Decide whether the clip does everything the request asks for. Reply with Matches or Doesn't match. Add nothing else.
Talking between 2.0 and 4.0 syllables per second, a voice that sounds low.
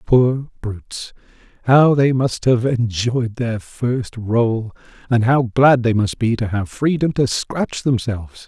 Matches